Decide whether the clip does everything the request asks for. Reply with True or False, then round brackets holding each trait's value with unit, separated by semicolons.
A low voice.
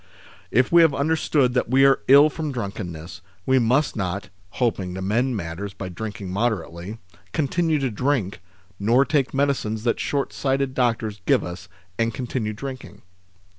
True (120 Hz)